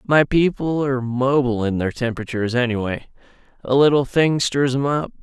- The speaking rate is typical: Yes, average, 150 wpm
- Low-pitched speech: Yes, low, 130 Hz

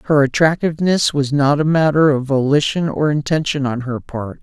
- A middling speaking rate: Yes, average, 175 wpm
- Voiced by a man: Yes, male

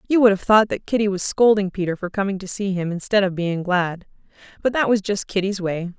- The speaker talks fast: Yes, fast, 240 wpm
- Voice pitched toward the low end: No, high, 195 Hz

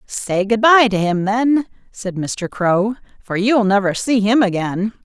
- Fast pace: No, average, 180 wpm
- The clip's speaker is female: Yes, female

